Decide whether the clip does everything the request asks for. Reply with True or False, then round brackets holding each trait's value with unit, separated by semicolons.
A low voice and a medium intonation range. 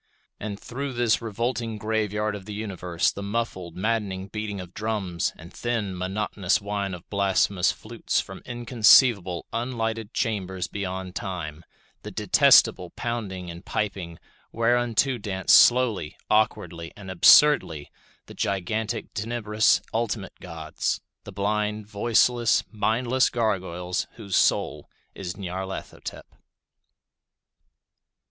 True (105 Hz; 3.3 semitones)